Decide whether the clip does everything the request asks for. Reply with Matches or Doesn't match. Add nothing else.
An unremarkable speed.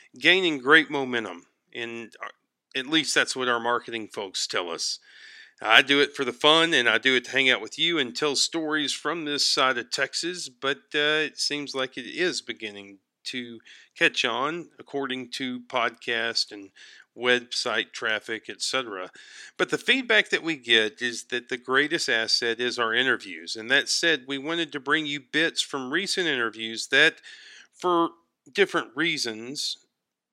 Matches